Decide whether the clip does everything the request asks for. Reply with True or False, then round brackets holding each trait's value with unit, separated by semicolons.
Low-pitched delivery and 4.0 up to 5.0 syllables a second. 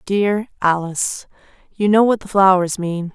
False (190 Hz; 4.4 syllables/s)